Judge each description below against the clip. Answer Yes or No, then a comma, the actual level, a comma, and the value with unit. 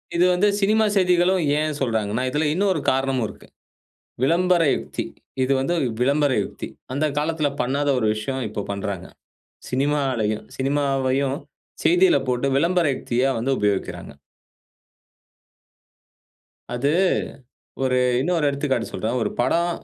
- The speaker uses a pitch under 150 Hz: Yes, medium, 140 Hz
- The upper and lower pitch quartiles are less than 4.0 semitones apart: No, average, 5.1 semitones